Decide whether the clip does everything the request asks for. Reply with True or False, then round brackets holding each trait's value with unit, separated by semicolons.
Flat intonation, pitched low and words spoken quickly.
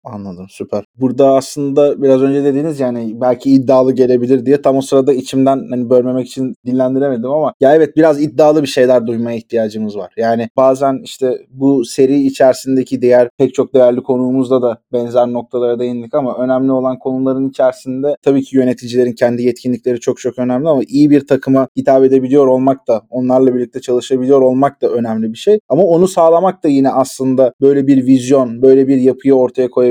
True (1.6 semitones; 130 Hz; 175 wpm)